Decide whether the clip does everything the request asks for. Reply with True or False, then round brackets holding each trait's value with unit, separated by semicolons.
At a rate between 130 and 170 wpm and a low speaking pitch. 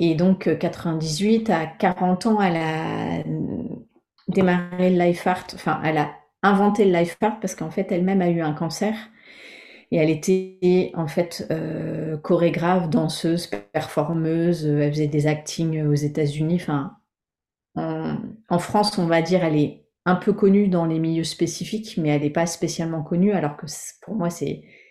False (165 wpm; 170 Hz)